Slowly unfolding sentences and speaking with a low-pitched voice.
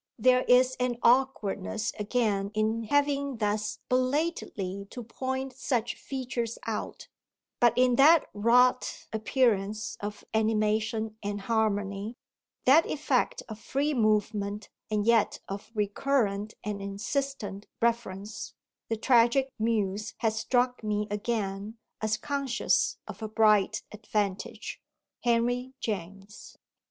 No: slow, 110 wpm; high, 220 Hz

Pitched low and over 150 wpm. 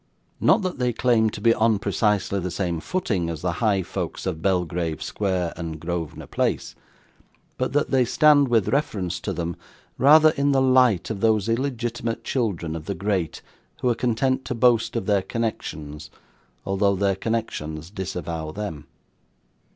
Yes: low, 105 Hz; average, 160 wpm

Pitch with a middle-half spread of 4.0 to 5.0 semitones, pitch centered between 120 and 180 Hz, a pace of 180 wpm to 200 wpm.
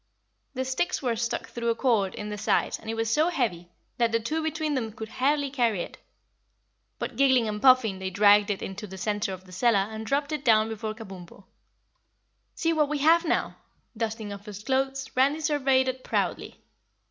No: average, 4.5 semitones; high, 230 Hz; average, 195 wpm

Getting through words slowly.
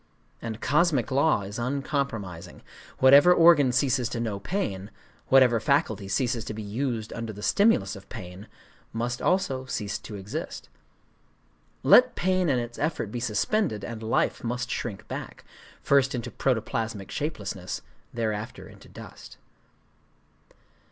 Yes: slow, 125 wpm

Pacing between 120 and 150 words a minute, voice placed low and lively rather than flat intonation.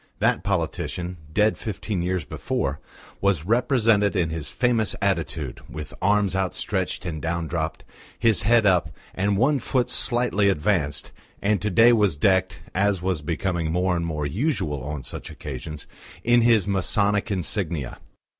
No: average, 145 wpm; very low, 95 Hz; average, 4.3 semitones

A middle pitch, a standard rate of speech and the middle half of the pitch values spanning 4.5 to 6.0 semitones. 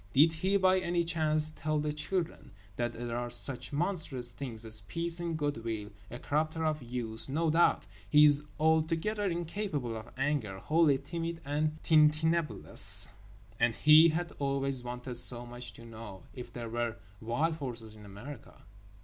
Yes: medium, 145 Hz; average, 160 wpm; average, 5.1 semitones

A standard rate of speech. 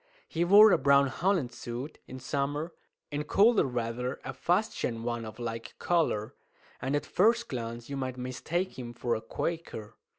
Yes: average, 165 wpm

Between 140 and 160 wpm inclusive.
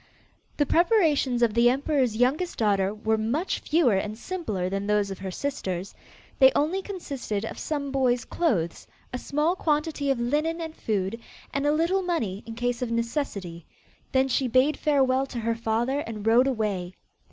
No: average, 170 wpm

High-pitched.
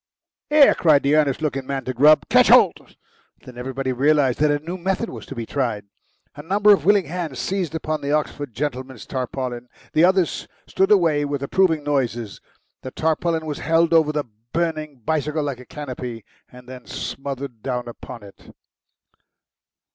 No: medium, 145 Hz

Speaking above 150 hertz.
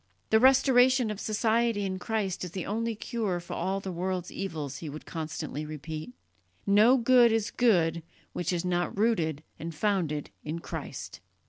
Yes: high, 190 Hz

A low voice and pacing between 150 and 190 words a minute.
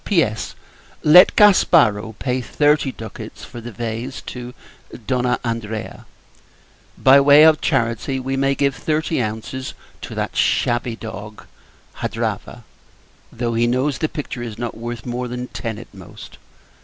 No: low, 125 Hz; average, 140 wpm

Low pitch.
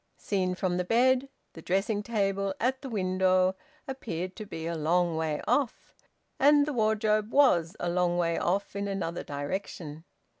No: high, 190 Hz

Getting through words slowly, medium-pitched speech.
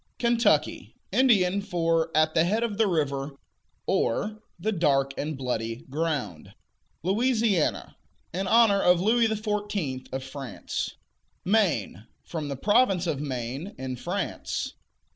Yes: slow, 125 wpm; medium, 170 Hz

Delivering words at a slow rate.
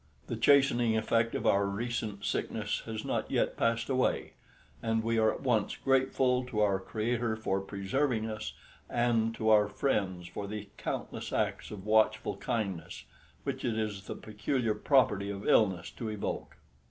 No: average, 160 wpm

